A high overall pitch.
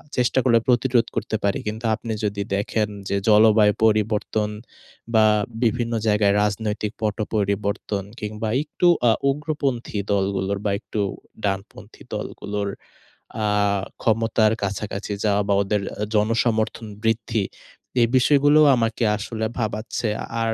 No: low, 110 Hz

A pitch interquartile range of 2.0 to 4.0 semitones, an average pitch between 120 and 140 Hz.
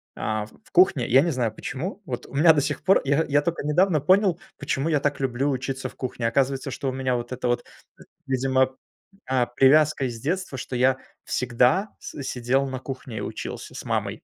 Yes: average, 2.8 semitones; low, 135 Hz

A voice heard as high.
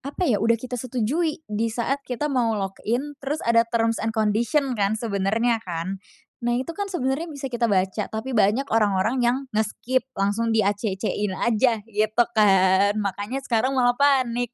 Yes: high, 230 Hz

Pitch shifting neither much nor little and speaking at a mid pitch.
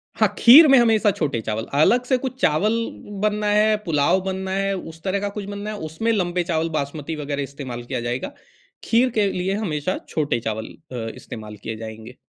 No: wide, 6.9 semitones; medium, 175 Hz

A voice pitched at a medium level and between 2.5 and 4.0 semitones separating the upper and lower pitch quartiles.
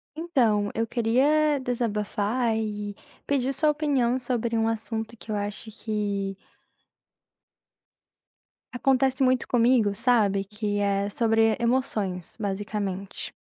No: high, 225 Hz; average, 3.6 semitones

